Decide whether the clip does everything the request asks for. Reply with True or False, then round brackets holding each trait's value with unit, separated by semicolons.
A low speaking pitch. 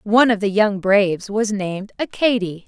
False (210 Hz)